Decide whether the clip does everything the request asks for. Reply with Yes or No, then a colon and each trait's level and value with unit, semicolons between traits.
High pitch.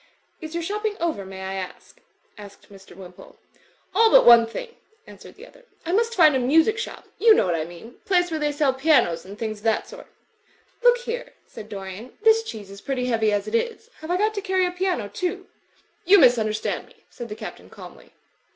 Yes: very high, 290 Hz